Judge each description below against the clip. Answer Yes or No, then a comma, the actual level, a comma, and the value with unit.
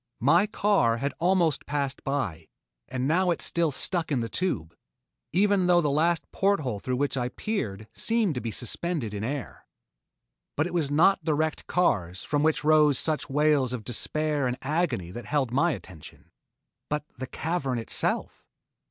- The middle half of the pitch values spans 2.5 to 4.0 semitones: No, wide, 5.5 semitones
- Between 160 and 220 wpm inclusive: Yes, average, 170 wpm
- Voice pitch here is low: No, medium, 145 Hz